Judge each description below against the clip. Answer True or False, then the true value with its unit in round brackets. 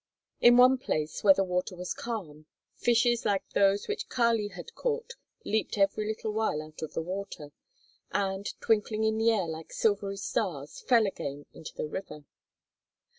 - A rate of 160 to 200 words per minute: True (165 wpm)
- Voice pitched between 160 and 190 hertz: False (200 Hz)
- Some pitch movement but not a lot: True (4.3 semitones)